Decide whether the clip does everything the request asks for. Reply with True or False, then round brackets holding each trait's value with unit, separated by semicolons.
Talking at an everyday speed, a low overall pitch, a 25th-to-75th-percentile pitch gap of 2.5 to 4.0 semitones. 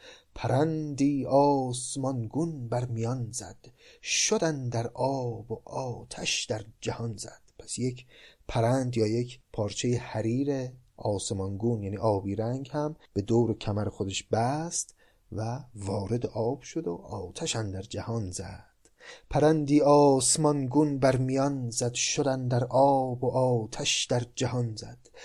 True (125 wpm; 125 Hz; 3.5 semitones)